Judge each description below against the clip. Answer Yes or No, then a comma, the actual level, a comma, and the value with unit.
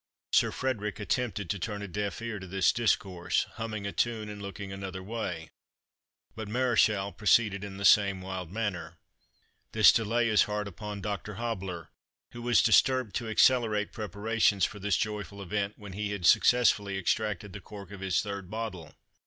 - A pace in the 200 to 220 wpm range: No, average, 170 wpm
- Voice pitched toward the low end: Yes, low, 105 Hz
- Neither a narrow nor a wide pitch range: No, narrow, 2.3 semitones